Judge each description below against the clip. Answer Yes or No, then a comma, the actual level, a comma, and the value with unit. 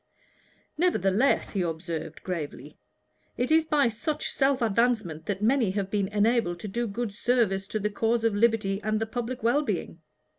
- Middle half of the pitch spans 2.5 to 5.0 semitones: Yes, average, 3.8 semitones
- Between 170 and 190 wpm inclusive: Yes, average, 175 wpm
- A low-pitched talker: No, high, 215 Hz